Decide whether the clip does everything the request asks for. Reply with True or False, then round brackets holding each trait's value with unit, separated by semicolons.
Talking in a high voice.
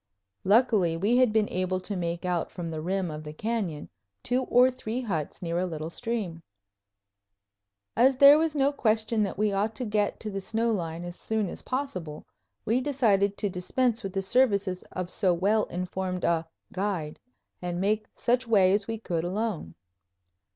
True (200 Hz)